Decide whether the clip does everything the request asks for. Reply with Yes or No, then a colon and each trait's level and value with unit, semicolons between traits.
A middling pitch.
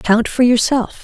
No: high, 240 Hz